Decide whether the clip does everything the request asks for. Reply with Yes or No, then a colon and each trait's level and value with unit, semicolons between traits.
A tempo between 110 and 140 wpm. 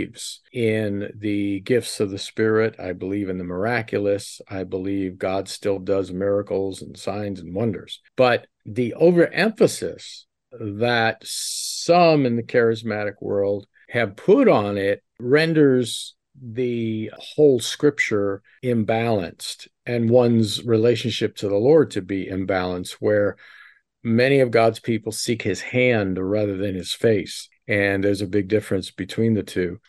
Yes: slow, 135 wpm